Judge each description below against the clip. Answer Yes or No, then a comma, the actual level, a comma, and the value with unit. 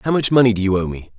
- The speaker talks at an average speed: No, fast, 355 wpm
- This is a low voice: Yes, low, 110 Hz